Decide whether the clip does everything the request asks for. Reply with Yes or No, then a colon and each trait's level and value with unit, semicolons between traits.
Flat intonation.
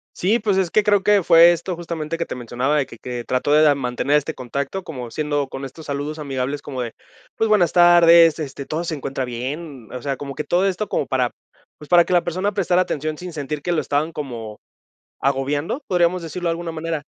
No: average, 4.2 semitones